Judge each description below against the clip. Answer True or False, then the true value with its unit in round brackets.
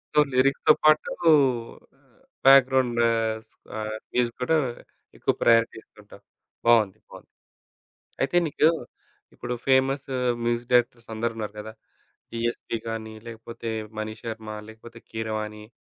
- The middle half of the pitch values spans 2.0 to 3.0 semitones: True (2.6 semitones)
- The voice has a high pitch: False (115 Hz)